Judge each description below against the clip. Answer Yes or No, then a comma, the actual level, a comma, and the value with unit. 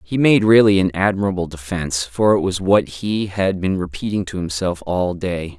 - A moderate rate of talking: Yes, average, 195 wpm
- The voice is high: No, very low, 95 Hz